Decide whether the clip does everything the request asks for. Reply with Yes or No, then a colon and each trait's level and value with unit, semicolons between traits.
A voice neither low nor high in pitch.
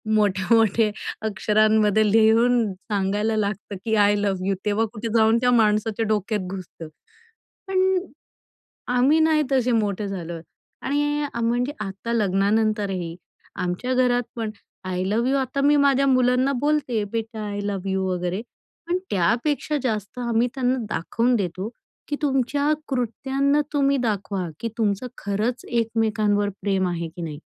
No: high, 220 Hz